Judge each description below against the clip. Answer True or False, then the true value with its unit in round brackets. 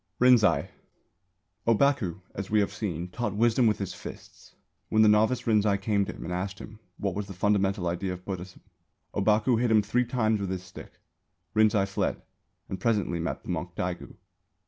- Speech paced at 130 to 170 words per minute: False (180 wpm)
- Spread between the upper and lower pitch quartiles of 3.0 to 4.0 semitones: False (2.6 semitones)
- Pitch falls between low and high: False (105 Hz)